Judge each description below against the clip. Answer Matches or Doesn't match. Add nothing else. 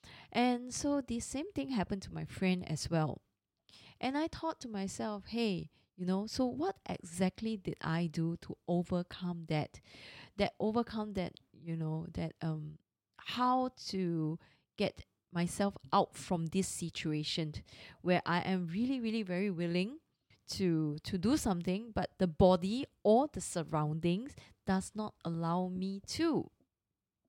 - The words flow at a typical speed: Matches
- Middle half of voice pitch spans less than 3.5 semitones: Doesn't match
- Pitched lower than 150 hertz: Doesn't match